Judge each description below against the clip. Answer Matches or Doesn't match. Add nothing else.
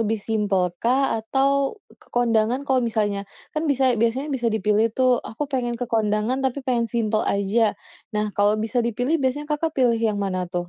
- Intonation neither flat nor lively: Matches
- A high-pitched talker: Matches